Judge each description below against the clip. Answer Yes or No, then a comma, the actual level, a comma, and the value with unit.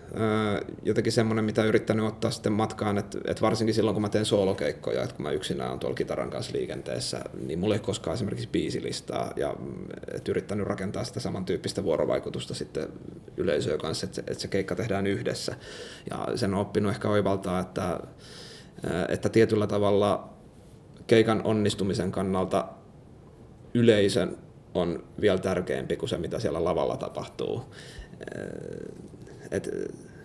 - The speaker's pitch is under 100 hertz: No, low, 105 Hz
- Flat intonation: Yes, narrow, 2.2 semitones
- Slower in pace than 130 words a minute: No, average, 135 wpm